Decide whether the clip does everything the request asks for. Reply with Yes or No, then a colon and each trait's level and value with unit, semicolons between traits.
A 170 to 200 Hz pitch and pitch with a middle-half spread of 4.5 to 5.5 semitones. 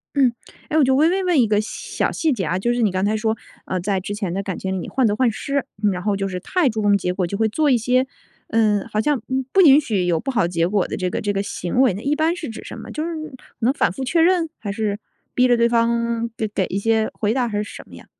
No: high, 220 Hz; average, 4.9 semitones